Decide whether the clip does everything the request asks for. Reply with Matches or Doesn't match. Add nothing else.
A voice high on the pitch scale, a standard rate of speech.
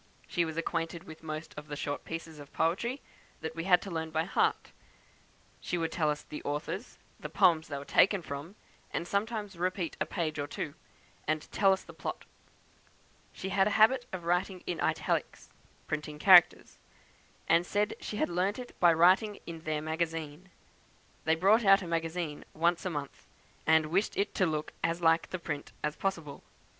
Doesn't match